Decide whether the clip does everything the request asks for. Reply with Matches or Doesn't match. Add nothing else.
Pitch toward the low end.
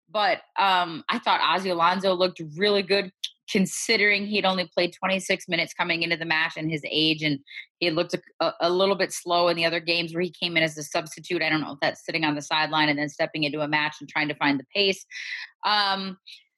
Doesn't match